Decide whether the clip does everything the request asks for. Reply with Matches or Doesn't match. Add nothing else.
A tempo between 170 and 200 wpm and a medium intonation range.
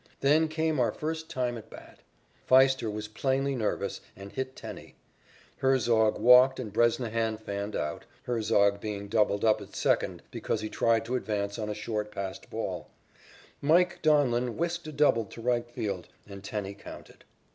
Doesn't match